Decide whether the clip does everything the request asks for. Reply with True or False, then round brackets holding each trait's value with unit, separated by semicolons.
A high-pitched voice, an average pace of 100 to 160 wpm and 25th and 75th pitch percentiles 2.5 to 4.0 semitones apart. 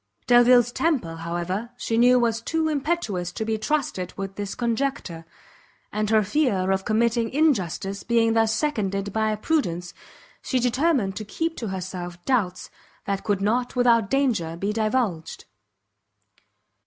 False (220 Hz; 140 wpm; 4.5 semitones)